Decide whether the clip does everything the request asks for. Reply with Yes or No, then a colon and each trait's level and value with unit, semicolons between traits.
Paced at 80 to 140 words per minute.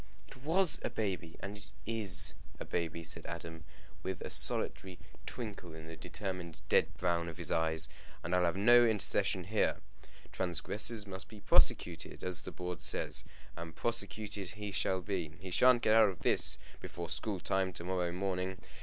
No: average, 170 wpm